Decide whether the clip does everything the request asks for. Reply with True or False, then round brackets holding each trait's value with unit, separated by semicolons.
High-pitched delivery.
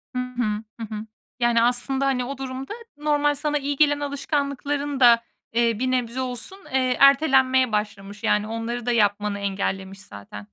True (250 Hz)